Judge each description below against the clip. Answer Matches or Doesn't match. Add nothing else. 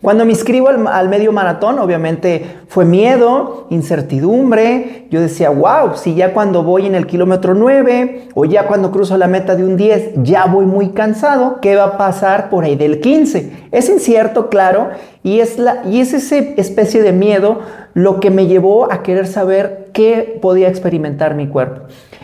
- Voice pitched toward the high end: Matches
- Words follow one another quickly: Doesn't match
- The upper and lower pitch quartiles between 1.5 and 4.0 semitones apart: Matches